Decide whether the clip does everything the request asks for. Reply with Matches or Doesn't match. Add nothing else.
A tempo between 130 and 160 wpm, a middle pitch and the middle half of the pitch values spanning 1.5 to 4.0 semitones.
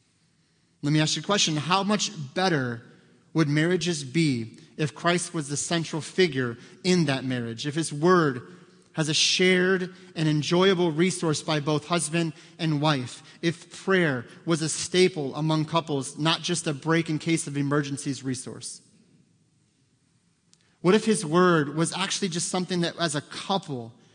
Matches